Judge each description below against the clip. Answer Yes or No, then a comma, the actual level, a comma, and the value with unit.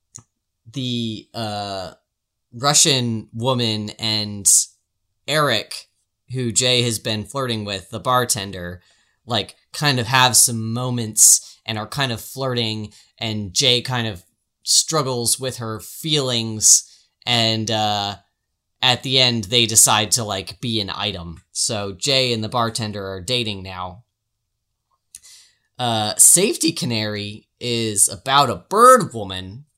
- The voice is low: Yes, low, 110 Hz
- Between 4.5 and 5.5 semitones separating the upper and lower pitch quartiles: No, average, 3.1 semitones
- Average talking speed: No, slow, 125 wpm